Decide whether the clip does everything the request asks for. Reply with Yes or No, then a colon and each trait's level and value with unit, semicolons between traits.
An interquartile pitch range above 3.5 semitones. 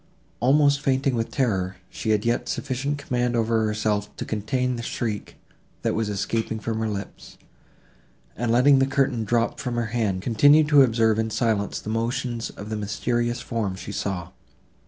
No: average, 2.9 semitones